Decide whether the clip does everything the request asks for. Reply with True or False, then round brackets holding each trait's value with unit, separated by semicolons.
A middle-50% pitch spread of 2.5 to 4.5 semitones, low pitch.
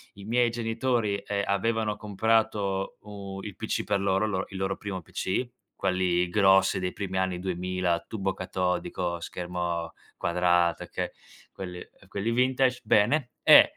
True (2.9 semitones; 95 Hz)